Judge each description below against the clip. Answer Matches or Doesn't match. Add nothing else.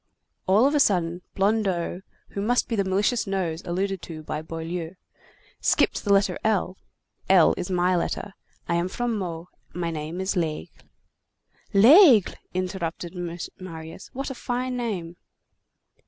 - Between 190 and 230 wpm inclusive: Doesn't match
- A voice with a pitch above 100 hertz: Matches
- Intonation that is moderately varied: Matches